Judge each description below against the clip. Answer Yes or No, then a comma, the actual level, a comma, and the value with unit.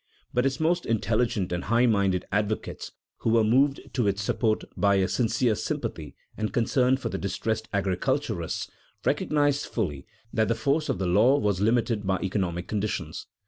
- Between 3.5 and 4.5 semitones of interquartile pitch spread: Yes, average, 3.9 semitones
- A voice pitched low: Yes, low, 110 Hz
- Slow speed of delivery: No, average, 165 wpm